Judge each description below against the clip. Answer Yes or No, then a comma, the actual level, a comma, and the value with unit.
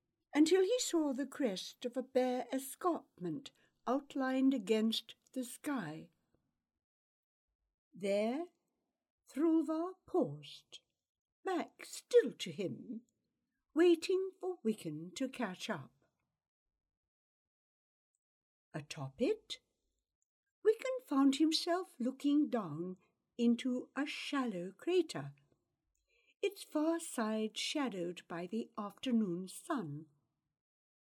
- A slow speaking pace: Yes, slow, 85 wpm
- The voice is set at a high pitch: Yes, high, 245 Hz